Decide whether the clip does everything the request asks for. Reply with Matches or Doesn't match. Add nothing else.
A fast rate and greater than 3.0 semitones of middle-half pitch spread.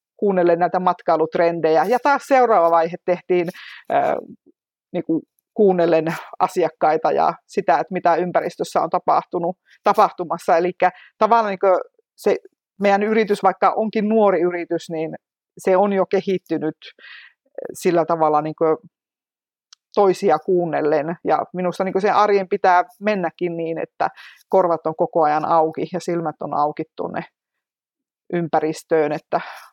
Doesn't match